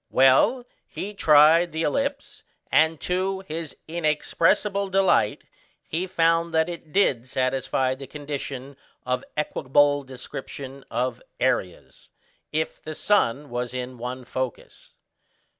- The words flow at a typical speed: No, slow, 115 wpm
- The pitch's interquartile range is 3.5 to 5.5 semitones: Yes, average, 4.5 semitones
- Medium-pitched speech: Yes, medium, 150 Hz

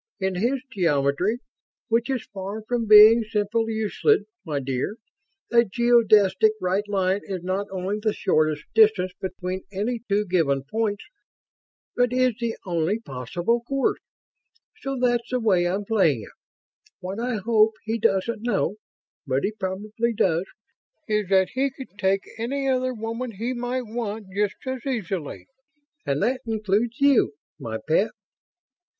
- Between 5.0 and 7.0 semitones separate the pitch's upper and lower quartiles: No, average, 3.9 semitones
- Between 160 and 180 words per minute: No, average, 145 wpm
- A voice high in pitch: Yes, high, 210 Hz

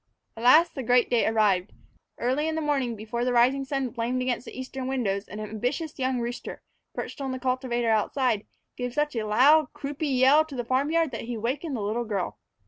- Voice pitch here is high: Yes, very high, 250 Hz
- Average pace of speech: No, fast, 210 wpm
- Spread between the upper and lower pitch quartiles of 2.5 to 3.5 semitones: Yes, average, 3.0 semitones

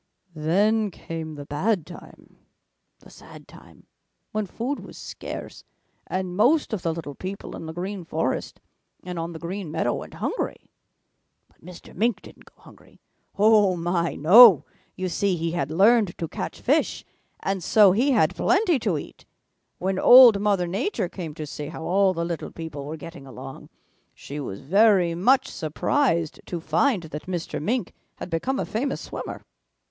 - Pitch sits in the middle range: Yes, medium, 180 Hz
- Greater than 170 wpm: No, average, 165 wpm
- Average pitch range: Yes, average, 4.5 semitones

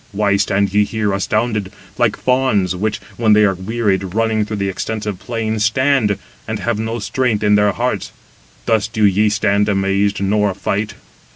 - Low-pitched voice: Yes, low, 105 Hz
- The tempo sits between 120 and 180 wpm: Yes, average, 170 wpm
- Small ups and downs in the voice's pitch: Yes, narrow, 1.9 semitones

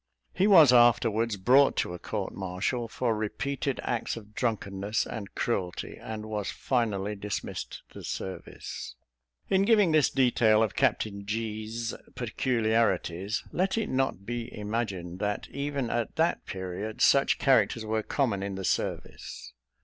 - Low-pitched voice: Yes, low, 110 Hz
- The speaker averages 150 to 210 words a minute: No, average, 140 wpm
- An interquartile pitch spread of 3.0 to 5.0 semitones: Yes, average, 3.9 semitones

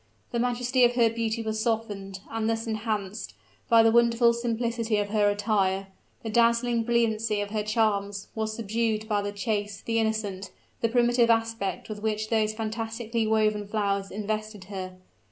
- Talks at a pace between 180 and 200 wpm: No, average, 160 wpm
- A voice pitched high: Yes, high, 220 Hz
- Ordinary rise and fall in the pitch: No, narrow, 1.9 semitones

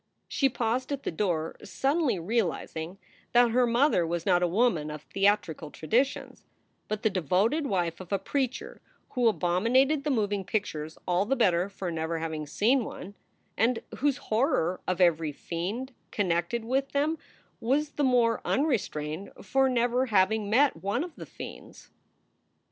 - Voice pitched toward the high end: Yes, high, 215 Hz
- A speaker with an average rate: Yes, average, 155 wpm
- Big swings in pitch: Yes, wide, 6.6 semitones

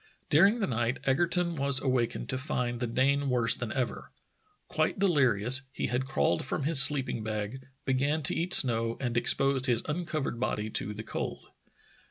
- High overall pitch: No, low, 130 Hz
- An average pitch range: Yes, average, 3.2 semitones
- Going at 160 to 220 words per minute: Yes, average, 170 wpm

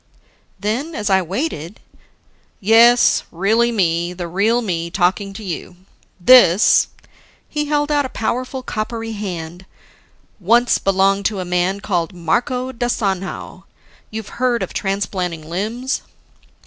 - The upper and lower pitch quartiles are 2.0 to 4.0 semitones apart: No, average, 4.9 semitones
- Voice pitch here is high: Yes, high, 200 Hz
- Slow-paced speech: Yes, slow, 125 wpm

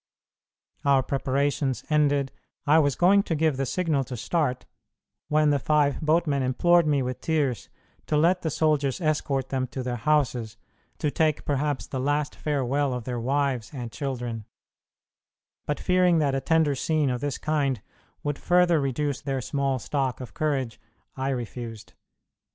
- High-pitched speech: No, medium, 140 Hz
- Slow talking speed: No, average, 155 wpm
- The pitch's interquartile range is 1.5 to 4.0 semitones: Yes, average, 2.9 semitones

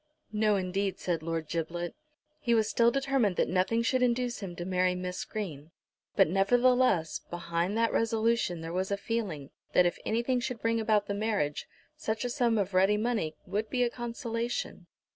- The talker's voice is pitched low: No, high, 210 Hz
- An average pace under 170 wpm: No, average, 180 wpm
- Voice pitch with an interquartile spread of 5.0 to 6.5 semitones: No, average, 4.5 semitones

